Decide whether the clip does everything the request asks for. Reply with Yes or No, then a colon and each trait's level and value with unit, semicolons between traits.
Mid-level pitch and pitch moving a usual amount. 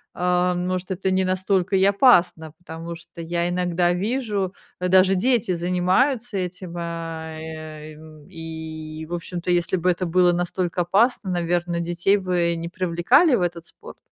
No: medium, 175 Hz; narrow, 1.8 semitones